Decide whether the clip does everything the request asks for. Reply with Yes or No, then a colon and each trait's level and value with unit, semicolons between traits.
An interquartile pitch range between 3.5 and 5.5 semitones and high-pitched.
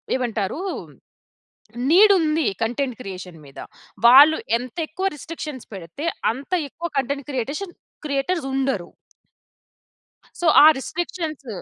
Yes: average, 4.9 semitones; very high, 280 Hz